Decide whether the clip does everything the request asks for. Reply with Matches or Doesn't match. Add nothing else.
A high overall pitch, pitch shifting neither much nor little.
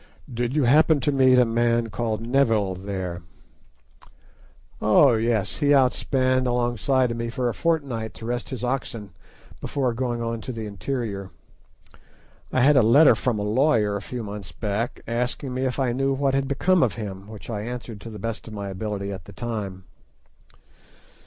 Doesn't match